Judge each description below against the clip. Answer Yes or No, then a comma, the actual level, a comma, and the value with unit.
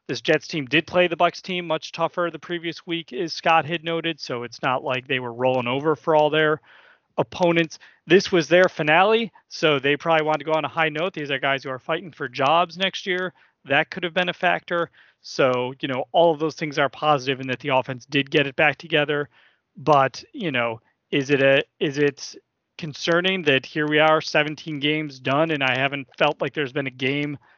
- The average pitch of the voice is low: No, medium, 155 Hz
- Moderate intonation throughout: Yes, average, 3.1 semitones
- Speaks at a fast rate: Yes, fast, 220 wpm